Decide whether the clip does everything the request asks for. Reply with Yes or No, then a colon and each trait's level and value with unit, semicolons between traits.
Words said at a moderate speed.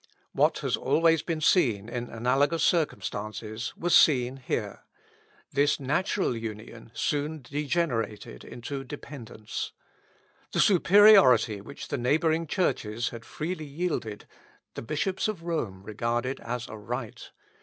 No: slow, 120 wpm